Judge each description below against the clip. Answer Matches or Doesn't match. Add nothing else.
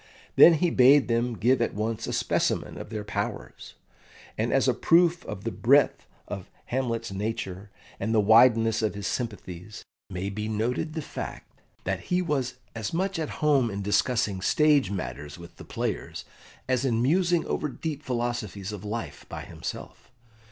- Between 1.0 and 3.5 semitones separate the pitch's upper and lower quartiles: Doesn't match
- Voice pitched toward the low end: Matches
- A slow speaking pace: Doesn't match